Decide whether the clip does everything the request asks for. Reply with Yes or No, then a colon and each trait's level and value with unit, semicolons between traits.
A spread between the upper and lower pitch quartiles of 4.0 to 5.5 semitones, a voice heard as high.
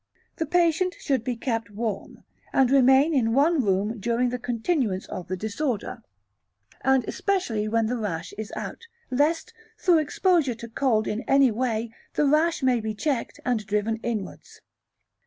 Yes: average, 4.6 semitones; high, 245 Hz